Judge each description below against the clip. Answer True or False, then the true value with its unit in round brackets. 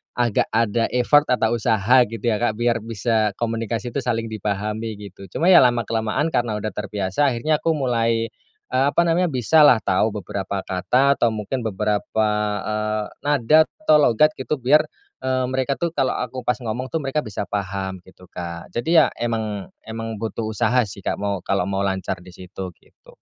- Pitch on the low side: True (115 Hz)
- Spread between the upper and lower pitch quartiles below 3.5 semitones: False (3.9 semitones)